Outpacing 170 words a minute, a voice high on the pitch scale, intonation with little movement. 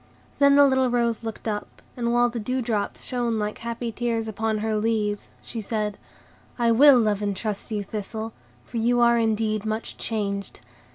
Yes: average, 180 wpm; high, 225 Hz; narrow, 2.0 semitones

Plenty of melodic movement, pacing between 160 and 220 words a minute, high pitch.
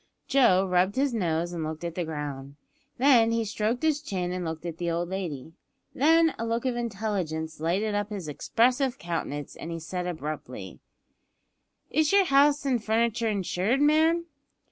Yes: wide, 7.0 semitones; average, 165 wpm; high, 200 Hz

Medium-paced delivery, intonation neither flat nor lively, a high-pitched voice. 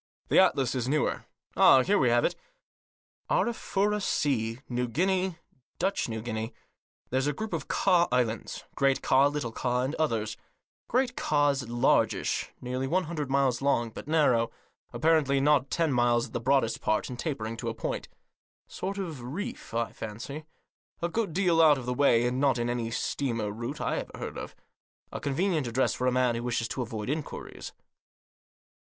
No: average, 180 wpm; average, 4.7 semitones; low, 135 Hz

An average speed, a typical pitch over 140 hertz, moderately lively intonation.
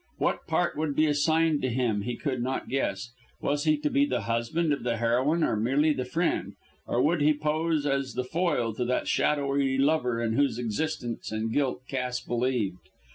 No: average, 190 wpm; low, 135 Hz; average, 3.9 semitones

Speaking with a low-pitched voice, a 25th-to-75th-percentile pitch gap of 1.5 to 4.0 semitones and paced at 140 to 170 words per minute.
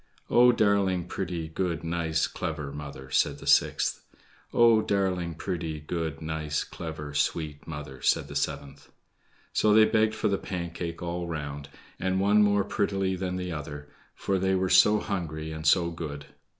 Yes: very low, 85 Hz; average, 3.7 semitones; average, 160 wpm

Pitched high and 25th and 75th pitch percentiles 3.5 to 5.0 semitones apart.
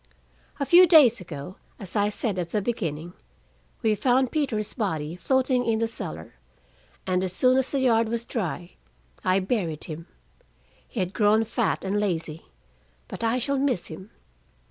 No: high, 210 Hz; wide, 5.4 semitones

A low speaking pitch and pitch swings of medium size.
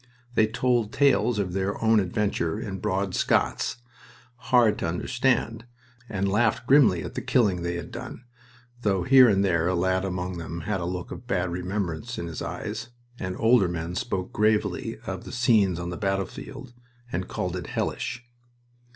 Yes: low, 100 Hz; average, 4.6 semitones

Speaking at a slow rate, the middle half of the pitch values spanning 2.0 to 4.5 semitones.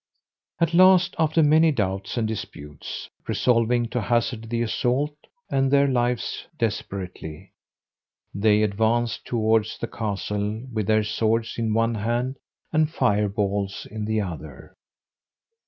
Yes: slow, 125 wpm; average, 3.0 semitones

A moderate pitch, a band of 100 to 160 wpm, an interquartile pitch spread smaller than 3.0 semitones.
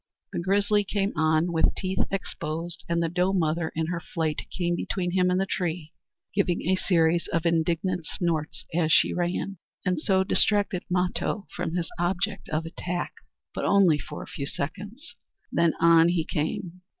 No: medium, 175 Hz; average, 170 wpm; narrow, 2.5 semitones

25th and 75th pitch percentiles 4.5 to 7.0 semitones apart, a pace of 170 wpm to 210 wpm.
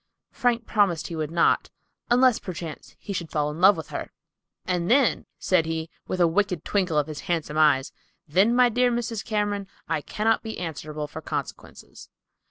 Yes: wide, 5.6 semitones; average, 180 wpm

